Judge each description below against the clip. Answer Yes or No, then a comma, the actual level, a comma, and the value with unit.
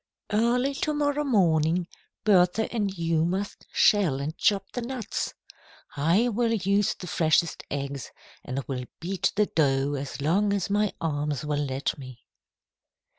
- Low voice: No, medium, 180 Hz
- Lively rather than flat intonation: Yes, wide, 6.2 semitones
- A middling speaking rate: Yes, average, 145 wpm